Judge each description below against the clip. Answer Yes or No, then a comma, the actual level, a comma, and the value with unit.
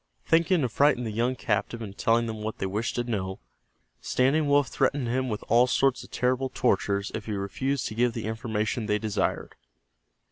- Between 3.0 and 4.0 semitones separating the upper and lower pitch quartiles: Yes, average, 3.3 semitones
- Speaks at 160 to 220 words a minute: Yes, average, 190 wpm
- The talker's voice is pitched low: Yes, low, 115 Hz